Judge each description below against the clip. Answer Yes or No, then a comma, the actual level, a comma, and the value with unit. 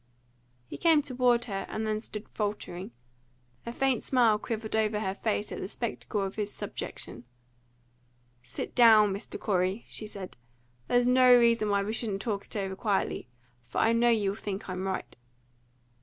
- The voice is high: Yes, high, 215 Hz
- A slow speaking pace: No, average, 170 wpm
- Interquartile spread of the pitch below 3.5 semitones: Yes, average, 3.0 semitones